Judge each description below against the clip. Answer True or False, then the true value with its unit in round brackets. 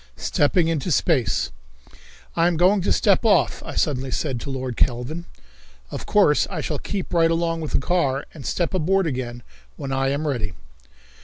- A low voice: False (155 Hz)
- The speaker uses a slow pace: False (175 wpm)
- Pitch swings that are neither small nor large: True (4.5 semitones)